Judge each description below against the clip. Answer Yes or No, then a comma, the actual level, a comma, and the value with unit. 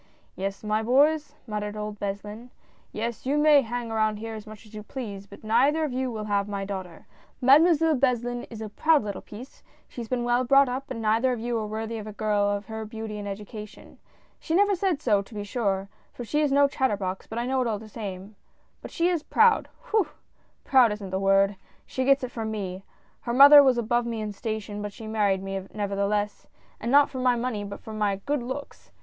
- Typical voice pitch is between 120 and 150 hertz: No, high, 220 Hz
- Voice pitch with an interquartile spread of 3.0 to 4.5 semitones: Yes, average, 3.9 semitones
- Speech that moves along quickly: Yes, fast, 240 wpm